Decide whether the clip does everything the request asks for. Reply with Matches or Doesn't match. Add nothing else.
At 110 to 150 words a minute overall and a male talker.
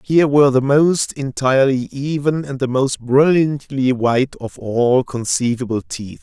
Matches